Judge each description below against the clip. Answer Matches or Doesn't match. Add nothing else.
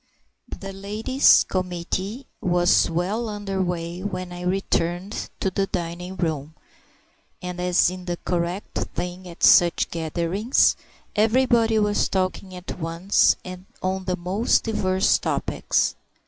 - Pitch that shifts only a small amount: Matches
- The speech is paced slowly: Matches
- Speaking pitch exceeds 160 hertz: Matches